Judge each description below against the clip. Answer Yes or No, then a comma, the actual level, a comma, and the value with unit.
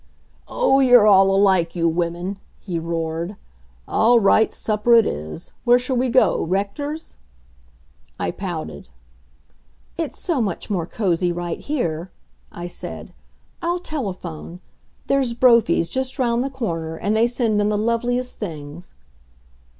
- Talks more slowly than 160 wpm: Yes, slow, 135 wpm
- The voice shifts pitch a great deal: Yes, wide, 6.1 semitones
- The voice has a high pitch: Yes, high, 210 Hz